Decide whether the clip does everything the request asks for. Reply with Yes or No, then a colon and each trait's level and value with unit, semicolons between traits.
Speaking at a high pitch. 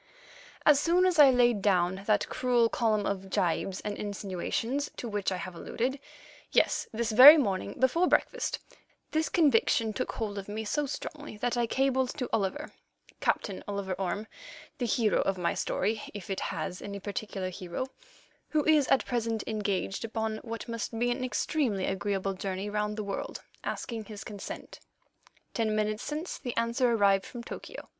Yes: high, 220 Hz